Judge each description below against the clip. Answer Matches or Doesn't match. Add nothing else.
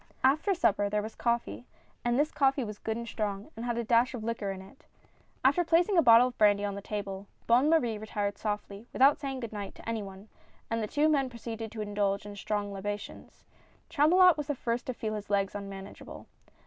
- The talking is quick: Matches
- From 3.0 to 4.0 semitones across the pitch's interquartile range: Doesn't match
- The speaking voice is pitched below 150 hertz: Doesn't match